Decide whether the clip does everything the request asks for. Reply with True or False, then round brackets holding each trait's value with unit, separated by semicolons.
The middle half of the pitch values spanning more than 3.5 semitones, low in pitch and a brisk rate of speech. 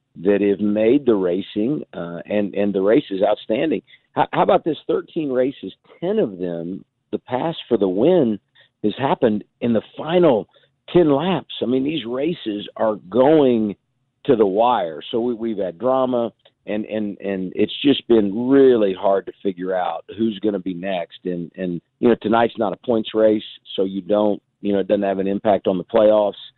False (3.9 semitones; 105 Hz; 190 wpm)